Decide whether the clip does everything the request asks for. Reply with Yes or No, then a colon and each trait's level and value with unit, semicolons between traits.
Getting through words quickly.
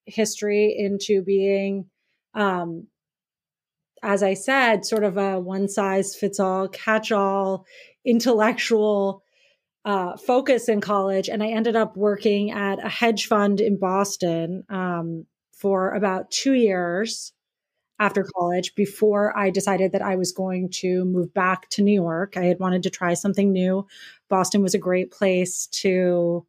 No: average, 145 wpm